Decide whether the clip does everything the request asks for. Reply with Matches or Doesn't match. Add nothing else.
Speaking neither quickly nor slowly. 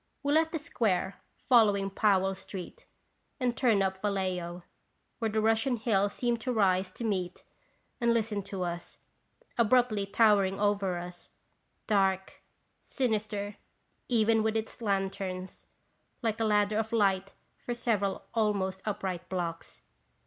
Doesn't match